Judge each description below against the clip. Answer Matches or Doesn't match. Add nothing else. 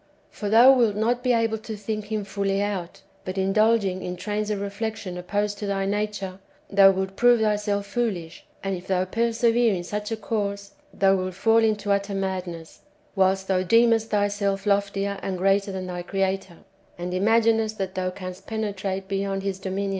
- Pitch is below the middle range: Doesn't match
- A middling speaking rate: Matches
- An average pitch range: Doesn't match